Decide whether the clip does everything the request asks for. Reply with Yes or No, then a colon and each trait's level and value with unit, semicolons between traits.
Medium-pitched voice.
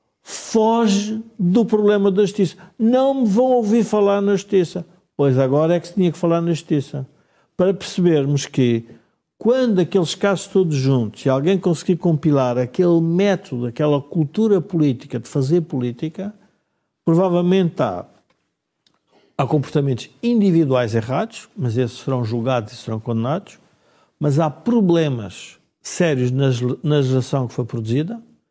Yes: medium, 165 Hz